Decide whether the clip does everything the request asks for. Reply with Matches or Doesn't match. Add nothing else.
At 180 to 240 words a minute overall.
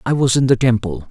Doesn't match